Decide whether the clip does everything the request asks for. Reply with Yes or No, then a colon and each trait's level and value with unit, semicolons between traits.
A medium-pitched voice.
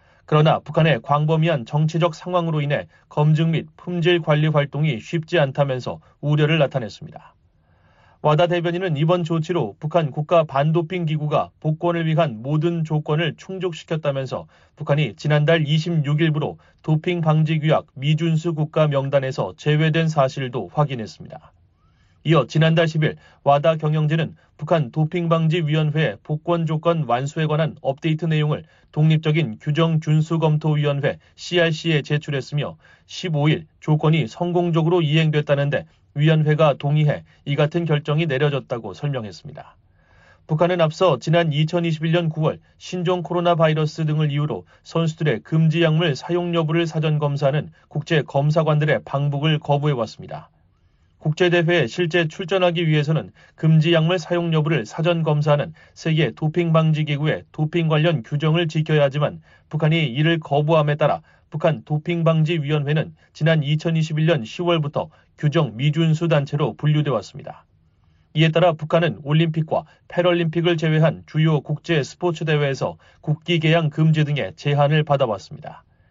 Yes: medium, 155 Hz